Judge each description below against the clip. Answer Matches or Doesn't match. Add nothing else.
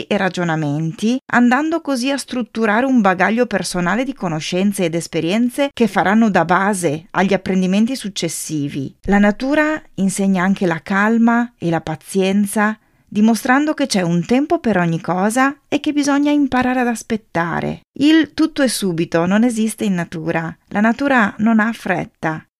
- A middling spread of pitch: Doesn't match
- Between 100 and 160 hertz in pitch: Doesn't match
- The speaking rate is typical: Matches